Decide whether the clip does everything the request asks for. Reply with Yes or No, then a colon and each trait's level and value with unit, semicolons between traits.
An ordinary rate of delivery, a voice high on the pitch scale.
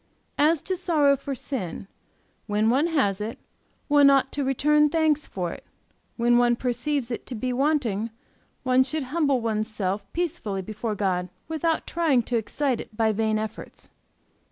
Yes: average, 160 wpm; very high, 255 Hz